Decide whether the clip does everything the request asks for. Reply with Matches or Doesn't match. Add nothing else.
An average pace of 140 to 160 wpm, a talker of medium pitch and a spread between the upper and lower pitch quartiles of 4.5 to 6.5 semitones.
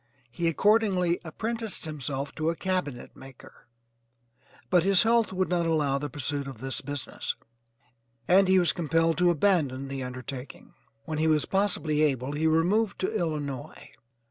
Matches